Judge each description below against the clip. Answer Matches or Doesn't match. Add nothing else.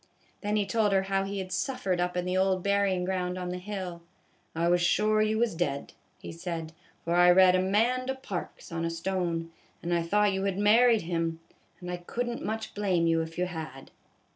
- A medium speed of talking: Doesn't match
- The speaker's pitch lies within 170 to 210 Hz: Matches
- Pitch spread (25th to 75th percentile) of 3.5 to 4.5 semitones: Doesn't match